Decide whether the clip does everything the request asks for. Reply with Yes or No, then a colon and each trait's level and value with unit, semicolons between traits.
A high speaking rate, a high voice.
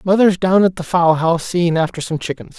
No: fast, 230 wpm; medium, 175 Hz